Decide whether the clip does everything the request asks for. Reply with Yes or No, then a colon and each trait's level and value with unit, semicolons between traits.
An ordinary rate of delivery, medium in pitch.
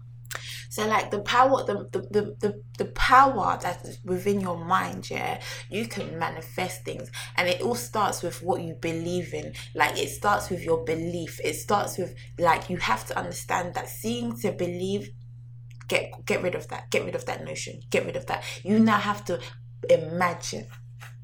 Yes: average, 185 wpm; medium, 165 Hz